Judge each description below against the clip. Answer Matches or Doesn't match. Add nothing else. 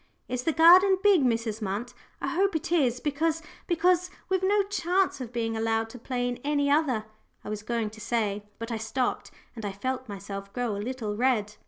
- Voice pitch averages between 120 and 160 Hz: Doesn't match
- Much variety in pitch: Matches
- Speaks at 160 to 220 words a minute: Matches